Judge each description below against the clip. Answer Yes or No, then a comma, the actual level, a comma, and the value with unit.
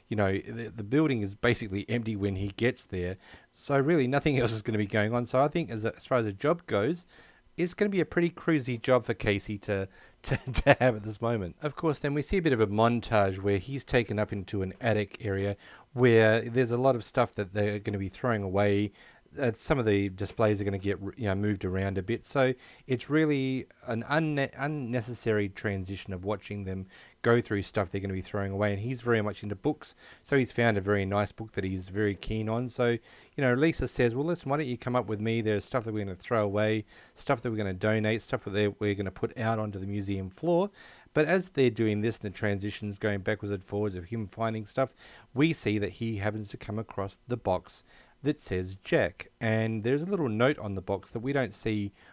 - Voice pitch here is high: No, low, 110 Hz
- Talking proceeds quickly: Yes, fast, 245 wpm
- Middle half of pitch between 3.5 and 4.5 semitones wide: Yes, average, 4.0 semitones